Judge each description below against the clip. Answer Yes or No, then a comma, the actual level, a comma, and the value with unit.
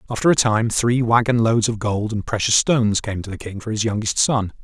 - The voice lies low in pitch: Yes, low, 110 Hz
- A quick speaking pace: Yes, fast, 245 wpm